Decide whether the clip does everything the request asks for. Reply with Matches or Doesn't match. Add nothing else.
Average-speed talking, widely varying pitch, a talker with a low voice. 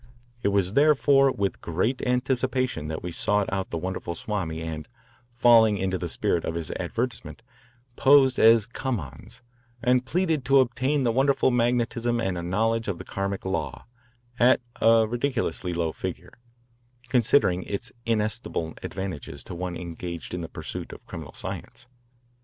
Matches